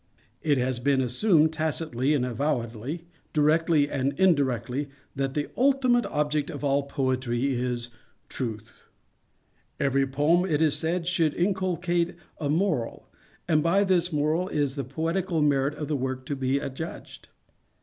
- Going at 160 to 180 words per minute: No, average, 140 wpm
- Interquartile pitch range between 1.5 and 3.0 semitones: No, average, 4.0 semitones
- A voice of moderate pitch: Yes, medium, 145 Hz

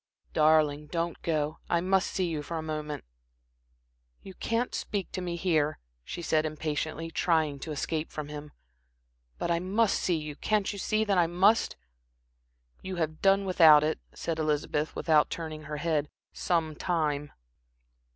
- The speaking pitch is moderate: Yes, medium, 160 Hz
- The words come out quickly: No, average, 160 wpm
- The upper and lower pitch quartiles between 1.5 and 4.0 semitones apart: Yes, average, 2.9 semitones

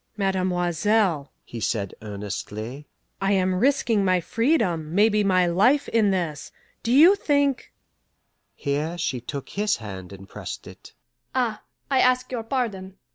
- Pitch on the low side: No, high, 190 Hz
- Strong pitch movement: Yes, wide, 7.4 semitones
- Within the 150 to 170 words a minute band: No, average, 140 wpm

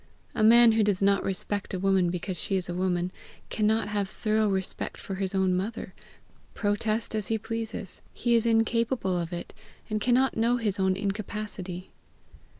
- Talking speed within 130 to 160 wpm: No, average, 170 wpm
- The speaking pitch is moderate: No, high, 205 Hz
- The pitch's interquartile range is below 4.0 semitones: Yes, average, 2.9 semitones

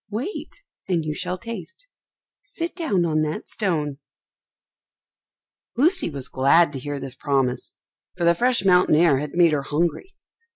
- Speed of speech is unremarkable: Yes, average, 150 wpm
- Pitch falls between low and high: Yes, medium, 170 Hz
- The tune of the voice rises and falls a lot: Yes, wide, 6.7 semitones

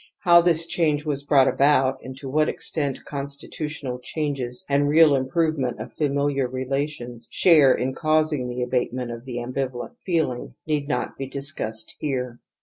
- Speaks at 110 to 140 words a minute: No, average, 155 wpm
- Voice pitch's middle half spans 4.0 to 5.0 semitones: No, average, 3.0 semitones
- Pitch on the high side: No, medium, 140 Hz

